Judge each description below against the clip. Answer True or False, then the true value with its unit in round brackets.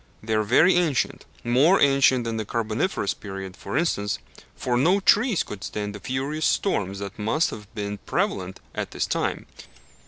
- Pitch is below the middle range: True (115 Hz)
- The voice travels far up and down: True (5.9 semitones)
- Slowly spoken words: False (165 wpm)